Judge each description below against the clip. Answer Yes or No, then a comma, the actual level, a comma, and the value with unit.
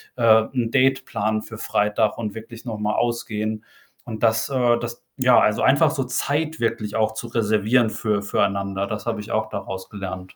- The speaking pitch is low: Yes, low, 110 Hz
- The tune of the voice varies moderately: No, narrow, 2.3 semitones